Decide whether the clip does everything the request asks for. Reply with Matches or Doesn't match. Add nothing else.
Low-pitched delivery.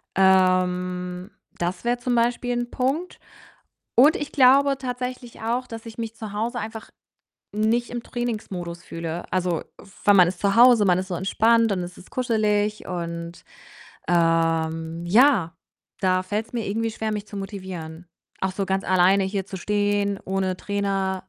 Doesn't match